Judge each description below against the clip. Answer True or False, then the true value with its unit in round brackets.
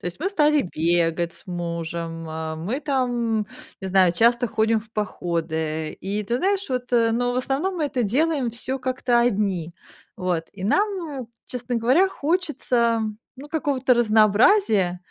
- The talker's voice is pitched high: True (230 Hz)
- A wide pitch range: True (6.9 semitones)